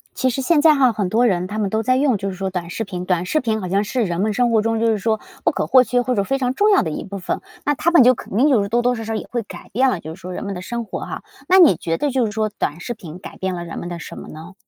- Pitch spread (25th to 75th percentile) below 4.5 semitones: No, average, 5.2 semitones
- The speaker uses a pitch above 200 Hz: Yes, high, 220 Hz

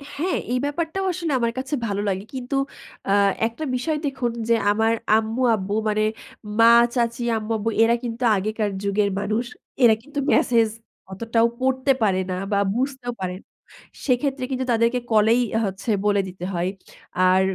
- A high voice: Yes, high, 230 Hz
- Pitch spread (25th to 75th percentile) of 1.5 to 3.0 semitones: No, average, 3.7 semitones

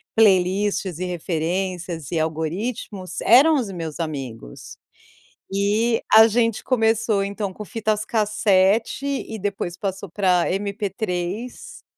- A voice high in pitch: Yes, high, 200 Hz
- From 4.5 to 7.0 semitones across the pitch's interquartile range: No, average, 3.7 semitones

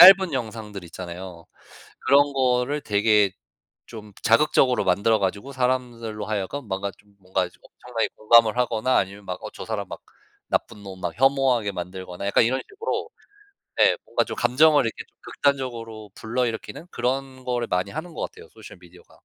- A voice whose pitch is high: No, low, 115 Hz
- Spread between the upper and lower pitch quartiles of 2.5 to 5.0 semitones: Yes, average, 4.5 semitones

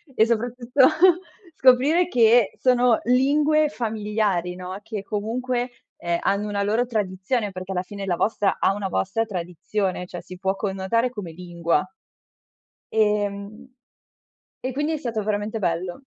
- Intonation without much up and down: No, average, 4.4 semitones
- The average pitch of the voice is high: Yes, high, 210 Hz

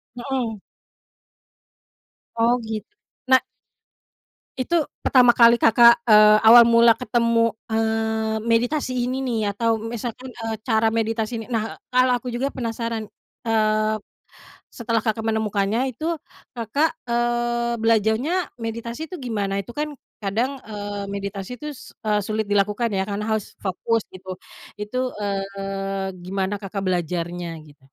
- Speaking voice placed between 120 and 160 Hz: No, high, 225 Hz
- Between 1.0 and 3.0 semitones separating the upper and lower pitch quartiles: Yes, average, 2.7 semitones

